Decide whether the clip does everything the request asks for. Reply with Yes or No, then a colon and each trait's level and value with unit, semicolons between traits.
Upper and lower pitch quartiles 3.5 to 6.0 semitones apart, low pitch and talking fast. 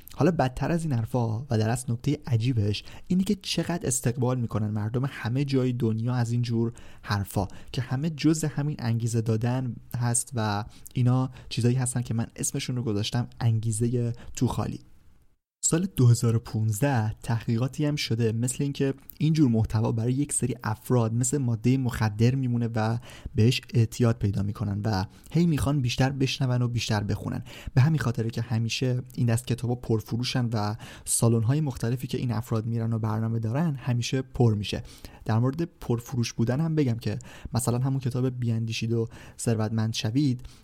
No: narrow, 2.6 semitones; low, 120 Hz; fast, 160 wpm